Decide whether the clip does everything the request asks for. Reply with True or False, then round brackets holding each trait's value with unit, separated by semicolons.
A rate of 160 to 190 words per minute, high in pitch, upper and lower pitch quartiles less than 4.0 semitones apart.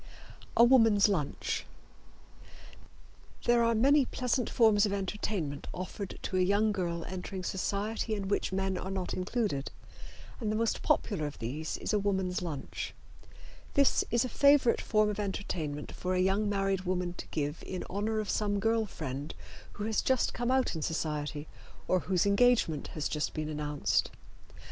False (165 wpm; 195 Hz; 4.4 semitones)